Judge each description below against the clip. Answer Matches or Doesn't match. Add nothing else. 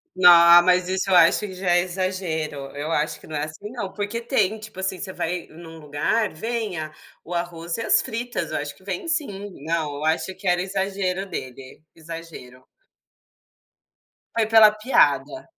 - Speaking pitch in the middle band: Matches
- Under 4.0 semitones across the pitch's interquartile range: Doesn't match